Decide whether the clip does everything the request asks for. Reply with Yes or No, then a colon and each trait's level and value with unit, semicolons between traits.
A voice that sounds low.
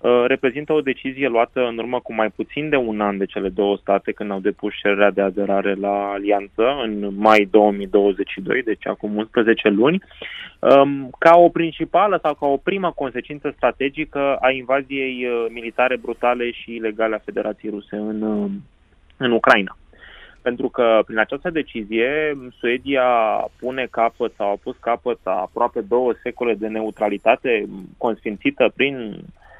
Yes: low, 115 Hz